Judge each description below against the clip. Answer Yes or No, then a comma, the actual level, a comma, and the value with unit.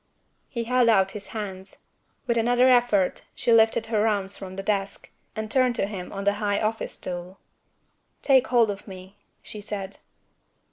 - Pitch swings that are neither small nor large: Yes, average, 3.0 semitones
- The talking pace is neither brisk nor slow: Yes, average, 170 wpm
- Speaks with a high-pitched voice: Yes, high, 210 Hz